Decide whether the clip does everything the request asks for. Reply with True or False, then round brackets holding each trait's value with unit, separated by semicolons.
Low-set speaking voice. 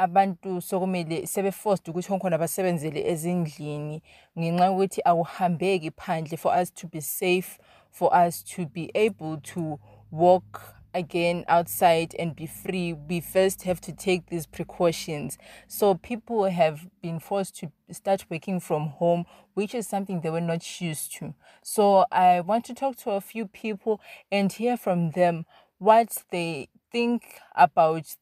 False (180 Hz)